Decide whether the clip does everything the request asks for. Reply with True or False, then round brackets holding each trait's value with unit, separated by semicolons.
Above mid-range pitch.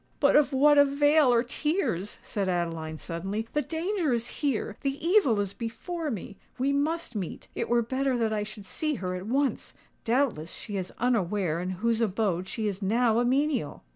True (230 Hz)